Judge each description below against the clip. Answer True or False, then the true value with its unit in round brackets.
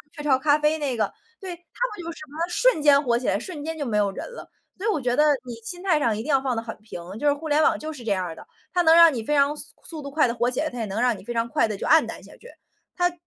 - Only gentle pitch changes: False (5.3 semitones)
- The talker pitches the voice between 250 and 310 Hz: True (290 Hz)